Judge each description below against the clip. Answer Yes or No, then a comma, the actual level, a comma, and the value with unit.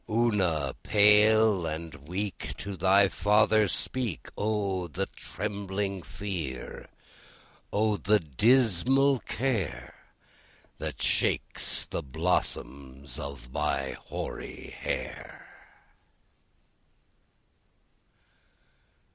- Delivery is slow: Yes, slow, 75 wpm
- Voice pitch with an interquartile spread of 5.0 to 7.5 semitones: Yes, wide, 5.6 semitones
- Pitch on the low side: Yes, very low, 95 Hz